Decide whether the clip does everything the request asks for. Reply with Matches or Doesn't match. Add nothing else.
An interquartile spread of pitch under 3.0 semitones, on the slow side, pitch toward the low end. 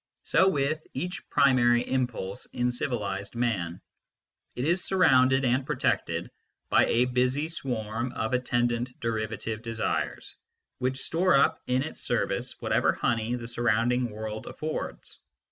Matches